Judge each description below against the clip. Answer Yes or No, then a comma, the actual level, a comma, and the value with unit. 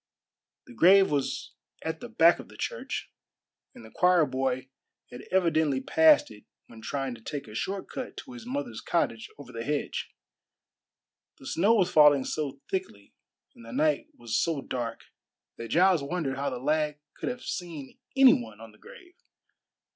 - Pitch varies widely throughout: Yes, wide, 6.5 semitones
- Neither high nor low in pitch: Yes, medium, 145 Hz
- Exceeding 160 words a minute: Yes, average, 170 wpm